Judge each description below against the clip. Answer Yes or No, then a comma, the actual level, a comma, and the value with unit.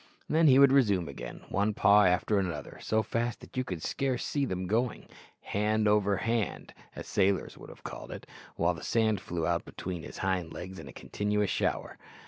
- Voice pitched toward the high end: No, low, 105 Hz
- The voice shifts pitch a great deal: No, average, 3.8 semitones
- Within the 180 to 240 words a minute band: Yes, average, 195 wpm